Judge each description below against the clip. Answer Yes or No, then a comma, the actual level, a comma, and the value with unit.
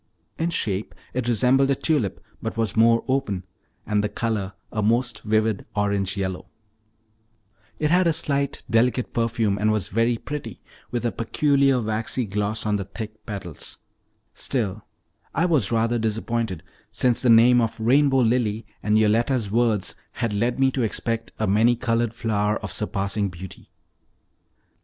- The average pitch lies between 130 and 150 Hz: No, low, 115 Hz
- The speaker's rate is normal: Yes, average, 150 wpm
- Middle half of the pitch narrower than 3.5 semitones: Yes, average, 2.8 semitones